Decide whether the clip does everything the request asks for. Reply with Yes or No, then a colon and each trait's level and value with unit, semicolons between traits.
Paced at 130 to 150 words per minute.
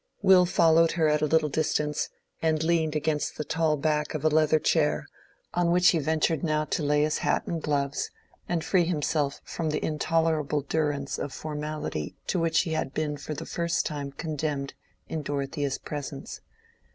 No: average, 175 wpm